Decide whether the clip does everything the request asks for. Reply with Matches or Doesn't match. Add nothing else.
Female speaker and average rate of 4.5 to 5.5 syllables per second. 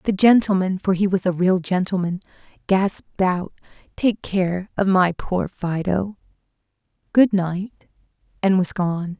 Doesn't match